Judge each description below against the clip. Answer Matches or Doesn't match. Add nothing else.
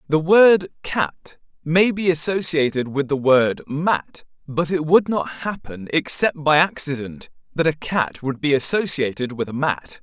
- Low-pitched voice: Doesn't match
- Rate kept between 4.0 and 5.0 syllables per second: Matches